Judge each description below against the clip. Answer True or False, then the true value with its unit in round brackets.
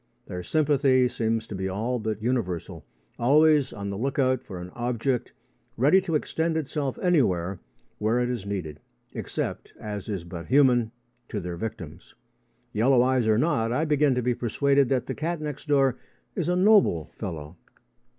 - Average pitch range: False (5.8 semitones)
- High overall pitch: False (120 Hz)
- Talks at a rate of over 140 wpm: True (170 wpm)